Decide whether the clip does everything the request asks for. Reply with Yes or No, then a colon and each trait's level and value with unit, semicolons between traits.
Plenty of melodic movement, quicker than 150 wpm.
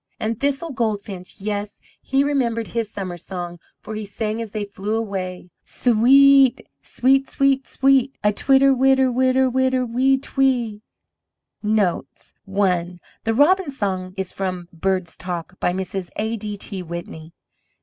No: wide, 5.7 semitones; average, 140 wpm